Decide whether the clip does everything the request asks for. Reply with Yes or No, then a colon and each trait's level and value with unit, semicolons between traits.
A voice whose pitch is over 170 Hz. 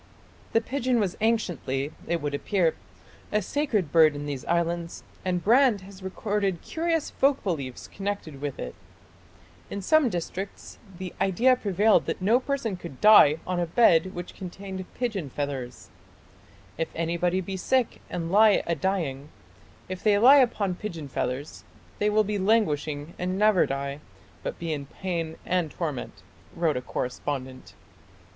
Yes: medium, 185 Hz